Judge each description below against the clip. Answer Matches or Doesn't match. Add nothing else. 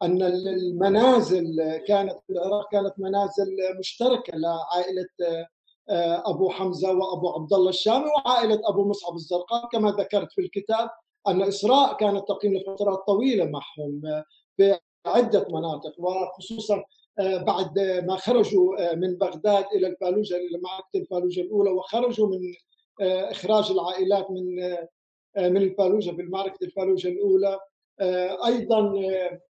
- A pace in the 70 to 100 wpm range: Doesn't match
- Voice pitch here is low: Doesn't match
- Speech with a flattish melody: Matches